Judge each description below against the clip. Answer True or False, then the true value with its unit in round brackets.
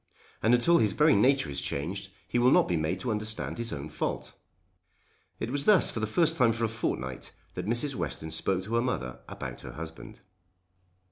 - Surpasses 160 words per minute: True (200 wpm)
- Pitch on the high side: False (110 Hz)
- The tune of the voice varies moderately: False (6.1 semitones)